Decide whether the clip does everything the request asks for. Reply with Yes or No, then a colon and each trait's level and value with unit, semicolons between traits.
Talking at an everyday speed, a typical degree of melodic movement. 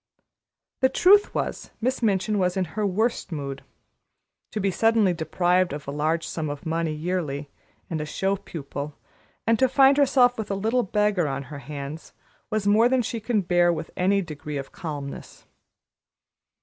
No: average, 170 wpm; wide, 6.2 semitones